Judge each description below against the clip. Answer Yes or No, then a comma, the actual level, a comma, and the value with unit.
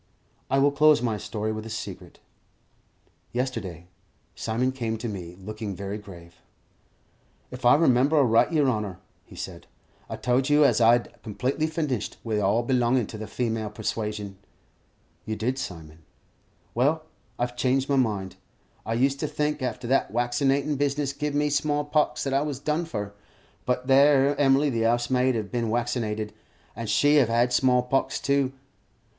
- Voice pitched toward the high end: No, low, 125 Hz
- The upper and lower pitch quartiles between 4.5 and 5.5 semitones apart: No, average, 4.1 semitones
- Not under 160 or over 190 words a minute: Yes, average, 165 wpm